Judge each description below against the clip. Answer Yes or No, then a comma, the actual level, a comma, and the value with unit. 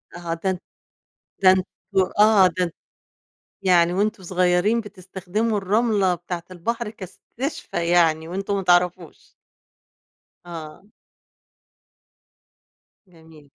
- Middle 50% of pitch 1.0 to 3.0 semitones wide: Yes, average, 2.7 semitones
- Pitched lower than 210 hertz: Yes, medium, 185 Hz